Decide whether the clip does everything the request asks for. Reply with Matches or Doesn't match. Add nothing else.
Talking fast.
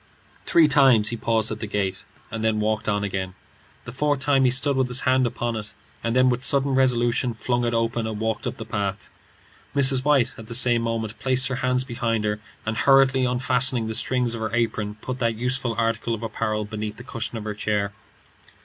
Matches